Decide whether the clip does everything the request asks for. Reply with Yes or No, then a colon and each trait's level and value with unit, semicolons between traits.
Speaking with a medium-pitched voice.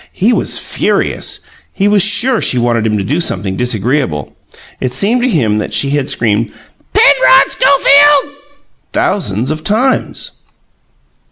Yes: medium, 150 Hz